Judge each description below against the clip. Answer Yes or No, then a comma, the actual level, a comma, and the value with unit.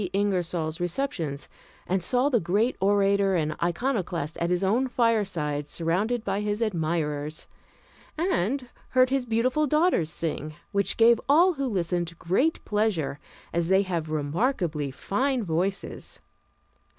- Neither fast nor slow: No, slow, 125 wpm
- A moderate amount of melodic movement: No, wide, 6.1 semitones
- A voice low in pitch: No, high, 195 Hz